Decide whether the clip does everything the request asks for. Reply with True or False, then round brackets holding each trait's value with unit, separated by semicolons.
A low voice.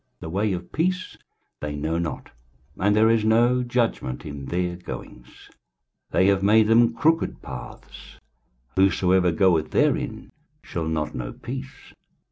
True (95 Hz)